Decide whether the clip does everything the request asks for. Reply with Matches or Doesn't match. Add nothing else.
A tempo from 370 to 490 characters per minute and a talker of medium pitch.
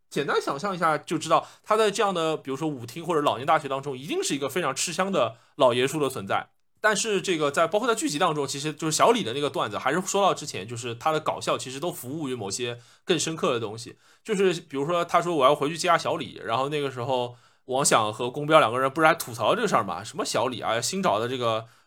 Matches